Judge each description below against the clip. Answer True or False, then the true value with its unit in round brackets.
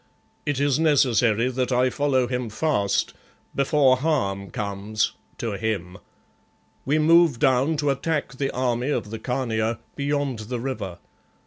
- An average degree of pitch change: True (4.4 semitones)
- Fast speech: False (135 wpm)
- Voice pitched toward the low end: True (130 Hz)